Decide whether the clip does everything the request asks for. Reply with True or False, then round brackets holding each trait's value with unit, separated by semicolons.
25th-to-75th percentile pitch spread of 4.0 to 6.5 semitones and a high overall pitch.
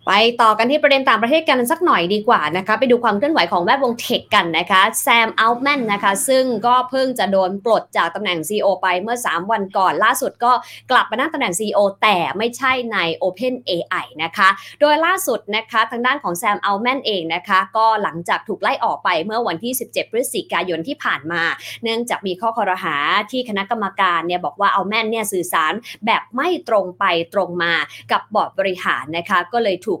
True (4.8 semitones; 220 Hz)